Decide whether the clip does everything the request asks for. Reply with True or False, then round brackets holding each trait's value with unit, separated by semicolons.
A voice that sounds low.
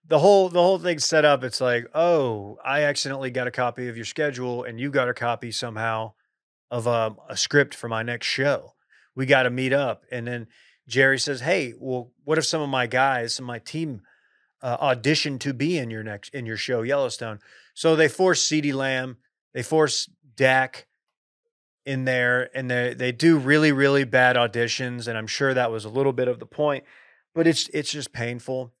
True (130 Hz)